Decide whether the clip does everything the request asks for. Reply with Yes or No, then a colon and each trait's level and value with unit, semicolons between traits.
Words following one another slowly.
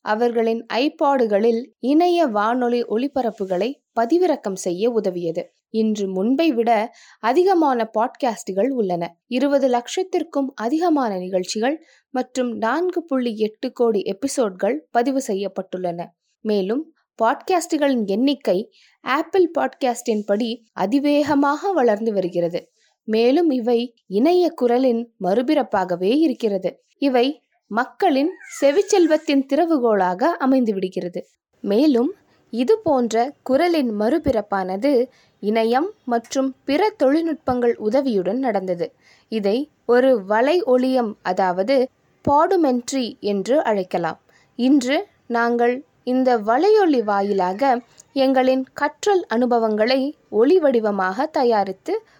Yes: slow, 85 wpm